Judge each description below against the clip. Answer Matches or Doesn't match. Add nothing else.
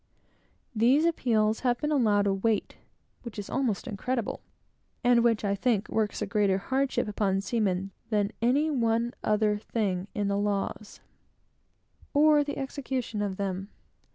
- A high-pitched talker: Matches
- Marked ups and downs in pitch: Doesn't match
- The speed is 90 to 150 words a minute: Matches